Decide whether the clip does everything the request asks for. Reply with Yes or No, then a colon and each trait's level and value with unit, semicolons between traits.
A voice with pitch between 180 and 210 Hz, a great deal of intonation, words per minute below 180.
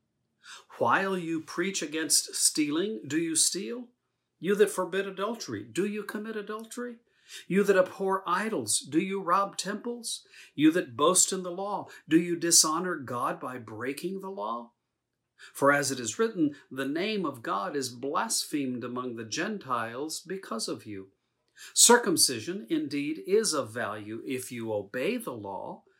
Yes: medium, 185 Hz; wide, 7.5 semitones; average, 150 wpm